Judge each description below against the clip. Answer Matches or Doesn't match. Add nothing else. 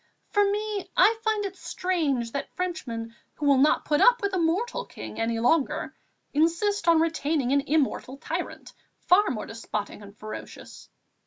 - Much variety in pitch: Matches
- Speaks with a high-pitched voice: Matches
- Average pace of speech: Matches